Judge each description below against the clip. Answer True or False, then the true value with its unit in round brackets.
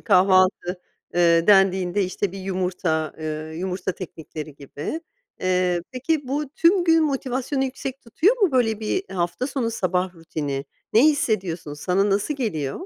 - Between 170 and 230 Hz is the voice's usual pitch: True (190 Hz)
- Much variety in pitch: True (7.0 semitones)